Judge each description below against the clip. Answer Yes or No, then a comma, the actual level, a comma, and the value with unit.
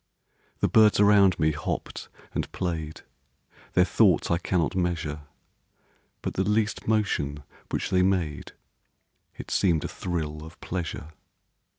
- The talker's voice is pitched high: No, very low, 90 Hz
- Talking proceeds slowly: Yes, slow, 125 wpm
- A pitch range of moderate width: Yes, average, 3.7 semitones